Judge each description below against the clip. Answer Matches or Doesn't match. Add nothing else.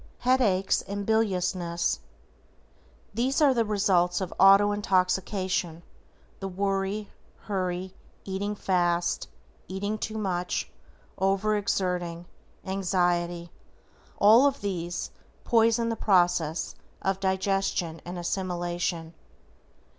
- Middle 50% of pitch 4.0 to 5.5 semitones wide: Doesn't match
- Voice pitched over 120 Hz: Matches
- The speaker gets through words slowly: Matches